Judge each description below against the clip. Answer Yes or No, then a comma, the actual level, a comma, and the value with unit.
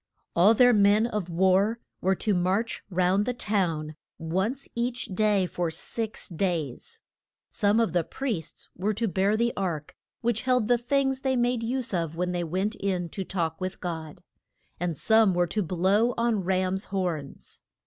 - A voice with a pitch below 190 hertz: No, high, 195 Hz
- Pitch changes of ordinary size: Yes, average, 4.4 semitones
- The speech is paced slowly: No, average, 170 wpm